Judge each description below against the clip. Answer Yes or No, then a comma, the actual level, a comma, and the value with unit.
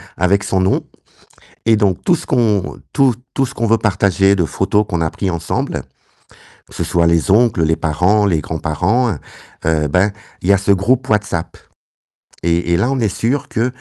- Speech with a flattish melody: No, average, 4.7 semitones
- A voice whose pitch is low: Yes, low, 100 Hz